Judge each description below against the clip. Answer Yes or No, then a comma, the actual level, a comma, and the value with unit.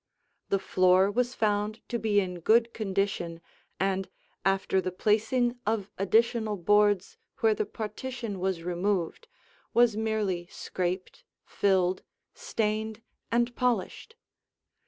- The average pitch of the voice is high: Yes, high, 205 Hz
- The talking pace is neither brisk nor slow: No, slow, 115 wpm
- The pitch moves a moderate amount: Yes, average, 3.0 semitones